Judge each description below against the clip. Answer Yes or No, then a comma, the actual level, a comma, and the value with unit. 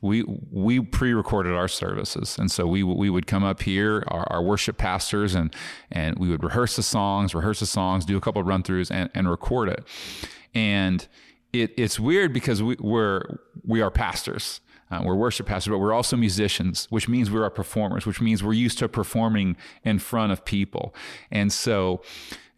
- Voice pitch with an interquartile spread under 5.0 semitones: Yes, average, 3.0 semitones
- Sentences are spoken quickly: No, average, 190 wpm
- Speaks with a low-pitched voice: Yes, low, 105 Hz